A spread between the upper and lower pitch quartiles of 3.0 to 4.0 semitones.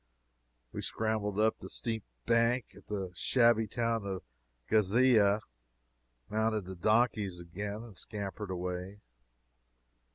No: narrow, 2.6 semitones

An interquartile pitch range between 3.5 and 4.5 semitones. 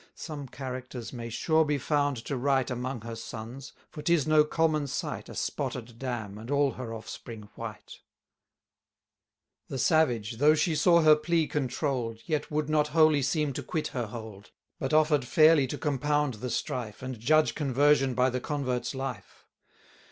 Yes: average, 3.9 semitones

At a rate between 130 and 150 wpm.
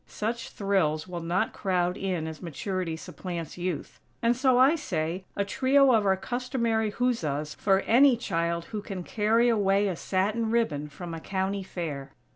No: average, 165 wpm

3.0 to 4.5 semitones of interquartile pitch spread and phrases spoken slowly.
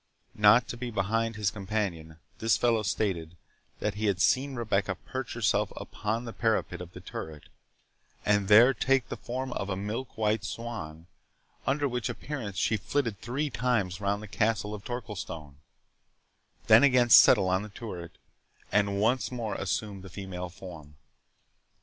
No: average, 3.6 semitones; average, 155 wpm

